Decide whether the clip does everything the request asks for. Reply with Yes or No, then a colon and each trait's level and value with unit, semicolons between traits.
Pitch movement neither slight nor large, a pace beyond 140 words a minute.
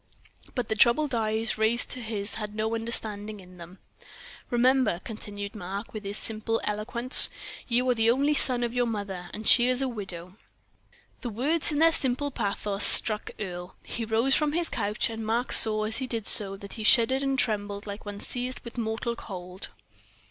Yes: average, 3.1 semitones; average, 185 wpm